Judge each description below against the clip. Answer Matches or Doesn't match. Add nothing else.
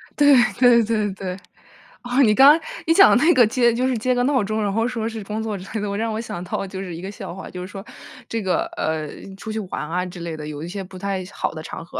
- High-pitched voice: Matches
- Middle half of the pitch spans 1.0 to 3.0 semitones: Doesn't match